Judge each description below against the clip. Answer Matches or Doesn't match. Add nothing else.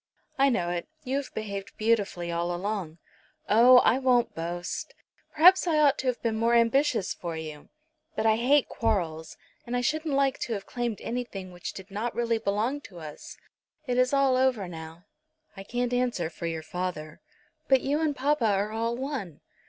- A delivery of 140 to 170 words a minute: Doesn't match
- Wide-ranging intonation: Matches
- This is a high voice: Matches